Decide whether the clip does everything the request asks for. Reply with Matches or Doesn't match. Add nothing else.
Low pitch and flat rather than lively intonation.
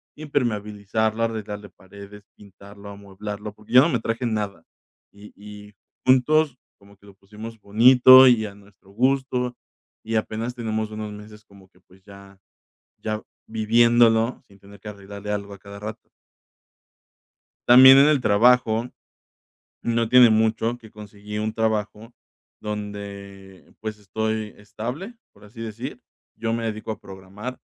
Matches